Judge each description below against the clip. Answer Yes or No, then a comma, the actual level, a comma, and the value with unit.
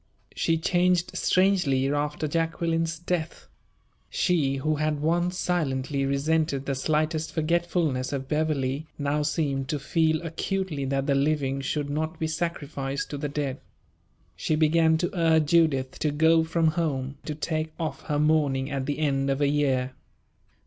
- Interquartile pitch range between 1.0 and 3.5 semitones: Yes, average, 2.8 semitones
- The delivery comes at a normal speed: Yes, average, 150 wpm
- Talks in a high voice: No, medium, 155 Hz